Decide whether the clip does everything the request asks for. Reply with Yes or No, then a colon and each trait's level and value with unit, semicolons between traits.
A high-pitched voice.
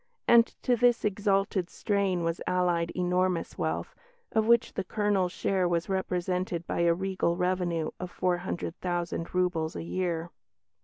No: medium, 180 Hz